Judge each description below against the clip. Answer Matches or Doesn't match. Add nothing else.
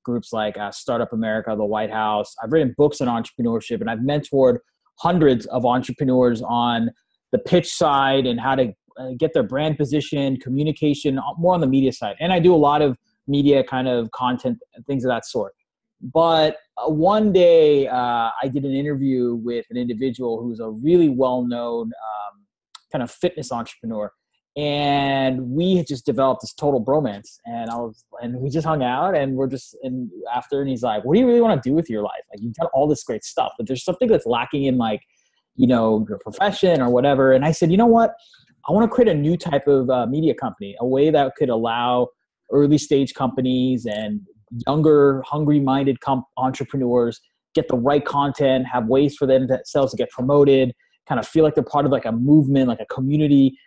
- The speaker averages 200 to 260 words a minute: Matches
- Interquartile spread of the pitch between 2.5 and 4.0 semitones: Matches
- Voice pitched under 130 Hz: Doesn't match